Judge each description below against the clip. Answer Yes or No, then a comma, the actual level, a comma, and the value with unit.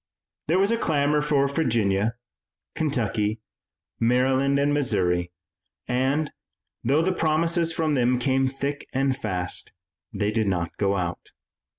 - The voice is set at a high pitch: No, low, 135 Hz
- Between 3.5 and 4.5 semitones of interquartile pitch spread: No, wide, 5.6 semitones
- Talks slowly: Yes, slow, 125 wpm